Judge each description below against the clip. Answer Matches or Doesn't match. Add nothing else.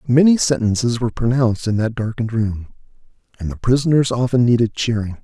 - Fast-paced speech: Doesn't match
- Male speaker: Matches